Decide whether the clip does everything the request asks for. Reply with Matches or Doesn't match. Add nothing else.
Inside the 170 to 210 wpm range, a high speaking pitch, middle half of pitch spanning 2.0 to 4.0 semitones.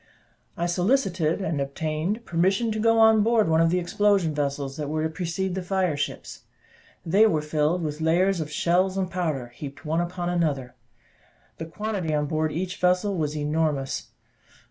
Doesn't match